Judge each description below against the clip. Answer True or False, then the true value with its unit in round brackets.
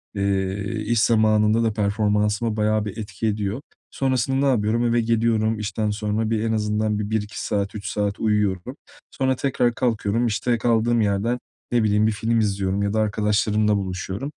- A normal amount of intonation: False (1.9 semitones)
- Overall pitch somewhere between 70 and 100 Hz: False (110 Hz)